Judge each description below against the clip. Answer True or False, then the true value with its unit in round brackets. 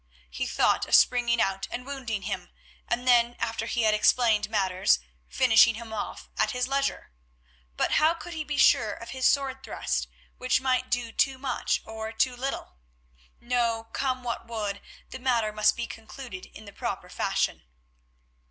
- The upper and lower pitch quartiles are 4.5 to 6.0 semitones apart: False (2.8 semitones)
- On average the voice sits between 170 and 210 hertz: False (235 Hz)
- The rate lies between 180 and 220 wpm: False (170 wpm)